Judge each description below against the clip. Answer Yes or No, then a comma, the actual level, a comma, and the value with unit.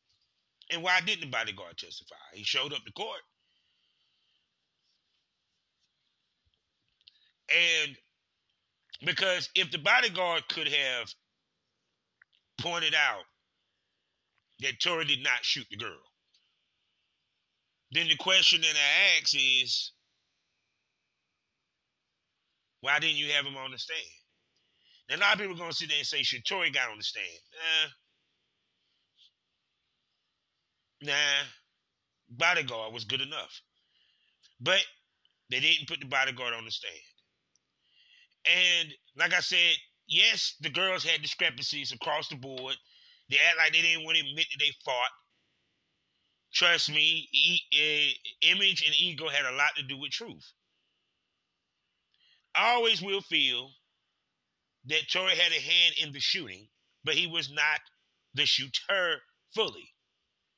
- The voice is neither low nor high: Yes, medium, 160 Hz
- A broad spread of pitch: No, average, 4.3 semitones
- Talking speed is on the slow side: Yes, slow, 130 wpm